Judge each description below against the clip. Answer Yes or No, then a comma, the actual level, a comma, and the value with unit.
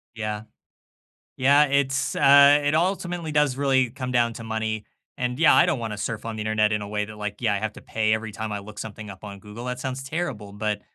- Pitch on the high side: No, low, 115 Hz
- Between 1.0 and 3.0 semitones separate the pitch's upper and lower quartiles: No, average, 4.5 semitones